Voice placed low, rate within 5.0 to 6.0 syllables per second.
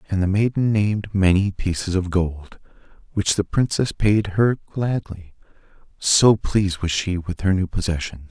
No: very low, 95 Hz; 4.6 syllables/s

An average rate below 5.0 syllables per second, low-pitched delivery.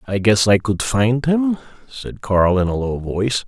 Yes: 4.3 syllables/s; low, 110 Hz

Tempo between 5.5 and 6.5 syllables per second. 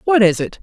Yes: 6.0 syllables/s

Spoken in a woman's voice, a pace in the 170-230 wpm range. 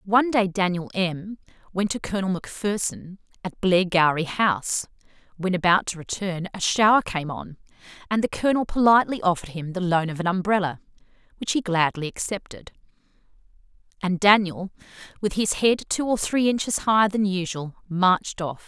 No: female; average, 155 wpm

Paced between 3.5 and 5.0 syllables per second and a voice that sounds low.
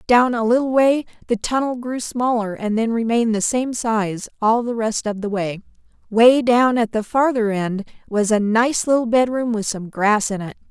No: 4.7 syllables/s; high, 230 Hz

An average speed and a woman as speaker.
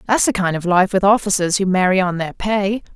No: fast, 245 wpm; female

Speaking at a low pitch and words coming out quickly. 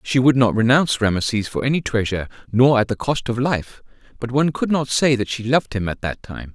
Yes: low, 120 Hz; fast, 240 wpm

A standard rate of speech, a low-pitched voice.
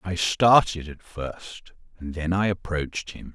Yes: average, 160 wpm; very low, 85 Hz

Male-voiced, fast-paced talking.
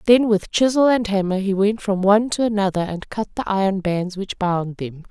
No: female; fast, 225 wpm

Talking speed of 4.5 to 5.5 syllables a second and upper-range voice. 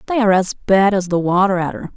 No: 6.6 syllables/s; high, 195 Hz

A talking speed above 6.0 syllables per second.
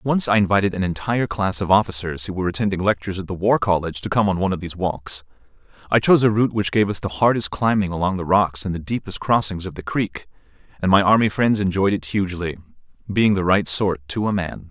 Yes: 6.4 syllables/s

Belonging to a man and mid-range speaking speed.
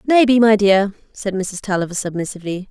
No: female; average, 155 wpm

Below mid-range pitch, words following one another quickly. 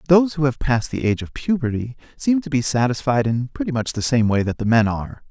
Yes: low, 130 Hz; fast, 250 wpm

